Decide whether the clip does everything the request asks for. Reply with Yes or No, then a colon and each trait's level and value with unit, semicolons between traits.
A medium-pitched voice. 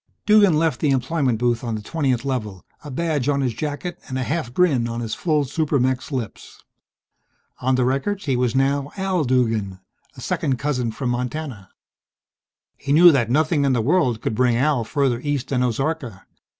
No: low, 130 Hz